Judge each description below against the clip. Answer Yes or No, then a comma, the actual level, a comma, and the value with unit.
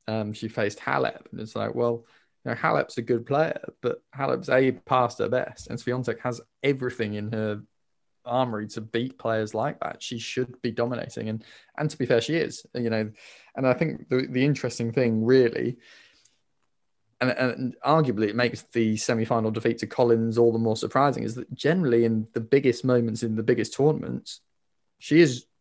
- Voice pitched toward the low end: Yes, low, 120 Hz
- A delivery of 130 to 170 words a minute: No, average, 185 wpm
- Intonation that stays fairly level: Yes, narrow, 2.3 semitones